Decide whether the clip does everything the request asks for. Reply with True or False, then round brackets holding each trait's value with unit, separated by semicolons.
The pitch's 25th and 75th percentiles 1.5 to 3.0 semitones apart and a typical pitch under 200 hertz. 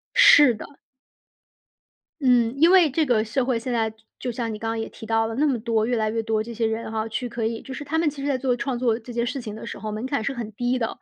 False (2.7 semitones; 235 Hz)